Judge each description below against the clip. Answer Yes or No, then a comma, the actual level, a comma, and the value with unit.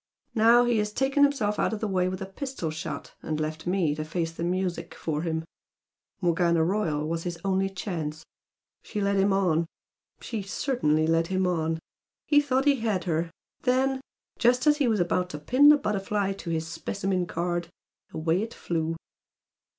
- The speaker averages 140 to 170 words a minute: No, average, 180 wpm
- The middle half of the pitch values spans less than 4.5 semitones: No, average, 4.9 semitones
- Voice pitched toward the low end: No, medium, 185 Hz